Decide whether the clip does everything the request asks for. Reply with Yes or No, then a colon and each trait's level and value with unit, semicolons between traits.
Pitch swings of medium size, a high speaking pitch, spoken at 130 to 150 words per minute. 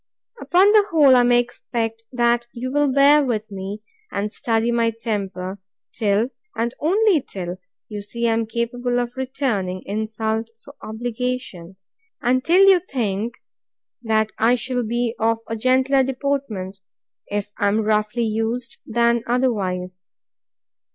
Yes: average, 3.1 semitones; high, 235 Hz; average, 140 wpm